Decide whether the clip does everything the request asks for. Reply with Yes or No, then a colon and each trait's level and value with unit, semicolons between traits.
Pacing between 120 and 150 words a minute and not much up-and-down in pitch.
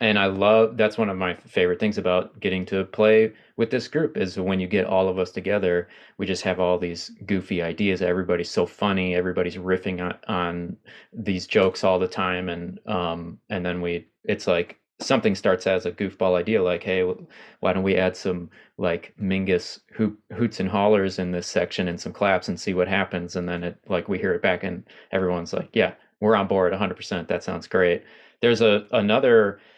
No: fast, 205 wpm; narrow, 1.9 semitones